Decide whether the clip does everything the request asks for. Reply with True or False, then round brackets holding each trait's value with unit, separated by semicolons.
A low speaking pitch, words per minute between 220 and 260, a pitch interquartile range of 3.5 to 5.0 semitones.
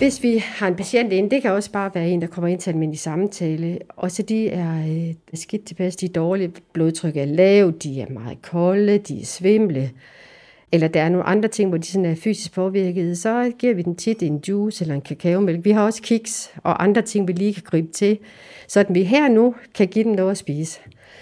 False (185 Hz; 225 wpm; 4.0 semitones)